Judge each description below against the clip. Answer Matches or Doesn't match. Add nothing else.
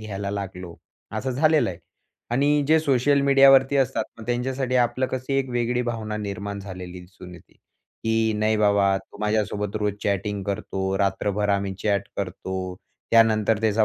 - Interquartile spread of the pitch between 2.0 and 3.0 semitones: Doesn't match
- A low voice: Matches